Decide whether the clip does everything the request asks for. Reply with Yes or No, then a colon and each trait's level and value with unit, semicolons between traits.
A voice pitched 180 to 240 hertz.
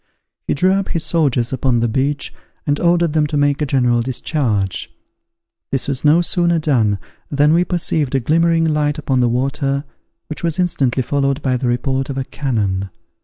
No: medium, 140 Hz